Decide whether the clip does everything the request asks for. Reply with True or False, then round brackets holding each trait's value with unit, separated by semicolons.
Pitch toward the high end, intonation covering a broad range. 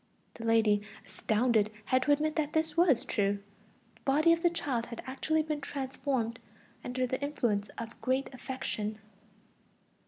False (260 Hz; 4.6 semitones)